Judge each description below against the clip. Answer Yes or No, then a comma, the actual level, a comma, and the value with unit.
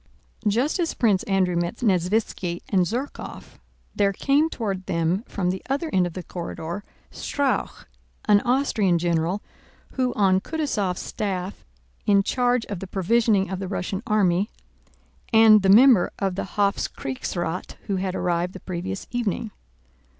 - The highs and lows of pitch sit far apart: No, average, 3.8 semitones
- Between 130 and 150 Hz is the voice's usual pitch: No, high, 195 Hz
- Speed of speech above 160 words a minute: No, average, 145 wpm